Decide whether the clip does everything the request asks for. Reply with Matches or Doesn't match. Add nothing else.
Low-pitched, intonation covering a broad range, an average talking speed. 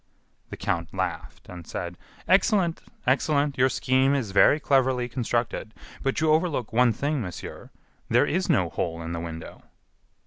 Matches